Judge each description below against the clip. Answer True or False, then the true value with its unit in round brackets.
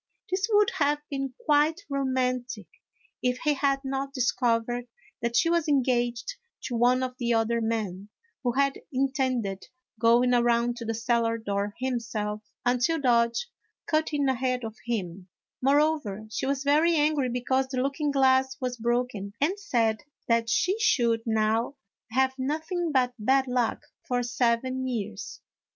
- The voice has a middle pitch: False (250 Hz)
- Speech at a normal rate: True (150 wpm)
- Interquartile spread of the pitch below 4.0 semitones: True (3.0 semitones)